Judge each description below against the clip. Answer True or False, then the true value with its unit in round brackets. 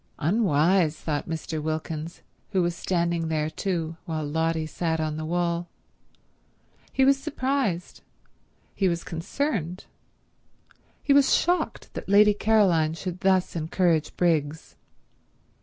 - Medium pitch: True (170 Hz)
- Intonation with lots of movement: False (3.3 semitones)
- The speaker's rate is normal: False (120 wpm)